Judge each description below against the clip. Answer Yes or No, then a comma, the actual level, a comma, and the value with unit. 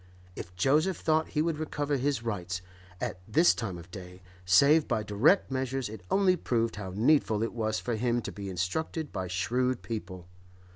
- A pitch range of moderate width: No, wide, 7.3 semitones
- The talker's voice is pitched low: Yes, low, 115 Hz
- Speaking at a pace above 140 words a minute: Yes, average, 180 wpm